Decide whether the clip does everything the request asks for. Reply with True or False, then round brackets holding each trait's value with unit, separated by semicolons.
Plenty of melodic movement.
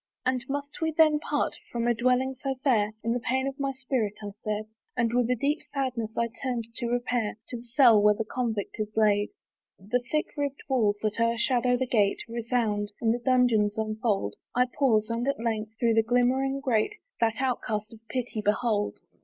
False (3.1 semitones)